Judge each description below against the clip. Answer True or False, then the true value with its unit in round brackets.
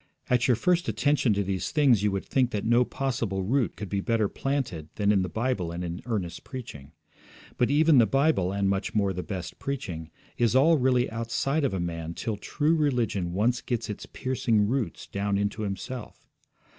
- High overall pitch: False (110 Hz)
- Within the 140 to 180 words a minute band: False (195 wpm)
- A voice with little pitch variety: False (5.1 semitones)